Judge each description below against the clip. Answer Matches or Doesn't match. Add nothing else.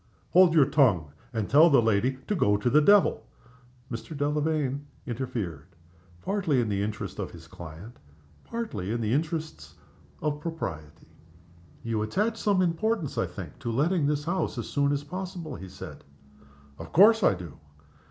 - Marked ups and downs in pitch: Matches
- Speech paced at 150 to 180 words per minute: Matches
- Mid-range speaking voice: Matches